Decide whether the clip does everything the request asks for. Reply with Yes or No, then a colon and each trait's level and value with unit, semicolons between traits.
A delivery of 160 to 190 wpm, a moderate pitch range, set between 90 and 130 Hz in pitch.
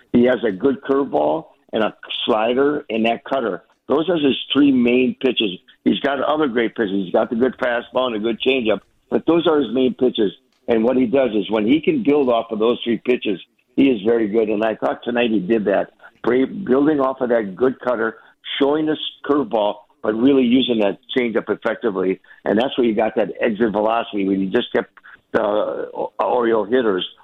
No: fast, 205 wpm; average, 3.3 semitones; low, 120 Hz